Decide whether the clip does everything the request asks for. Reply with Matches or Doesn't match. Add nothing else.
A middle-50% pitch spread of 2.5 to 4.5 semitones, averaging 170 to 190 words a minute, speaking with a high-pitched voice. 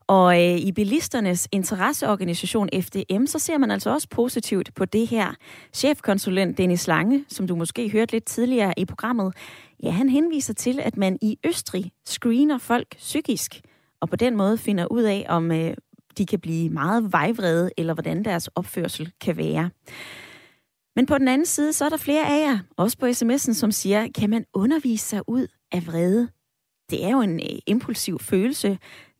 Doesn't match